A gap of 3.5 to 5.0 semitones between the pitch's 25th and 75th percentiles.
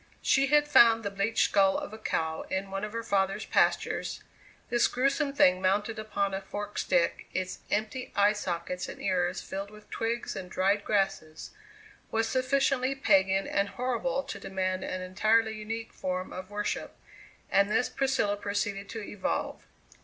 No: average, 3.0 semitones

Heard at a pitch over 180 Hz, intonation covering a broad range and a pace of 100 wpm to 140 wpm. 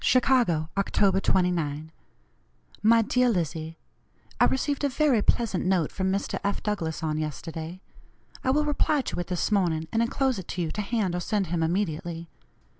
No: high, 190 Hz; wide, 5.9 semitones; average, 170 wpm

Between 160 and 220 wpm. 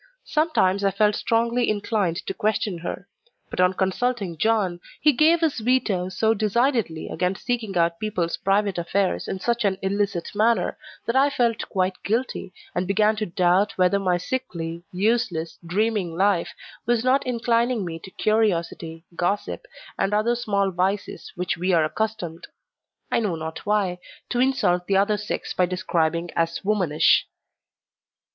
No: average, 150 wpm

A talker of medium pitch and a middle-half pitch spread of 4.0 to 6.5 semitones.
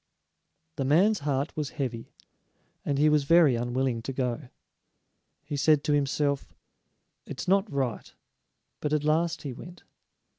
No: medium, 145 Hz; narrow, 2.5 semitones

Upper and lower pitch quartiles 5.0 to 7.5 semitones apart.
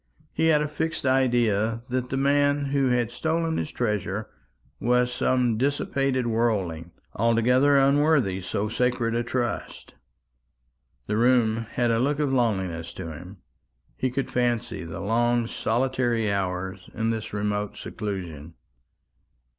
No: average, 4.0 semitones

